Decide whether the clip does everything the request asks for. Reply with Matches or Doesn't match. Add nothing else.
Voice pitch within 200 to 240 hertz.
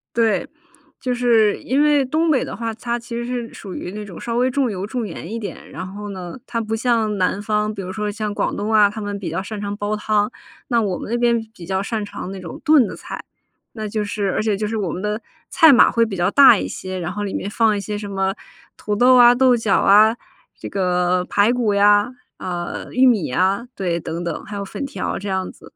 Matches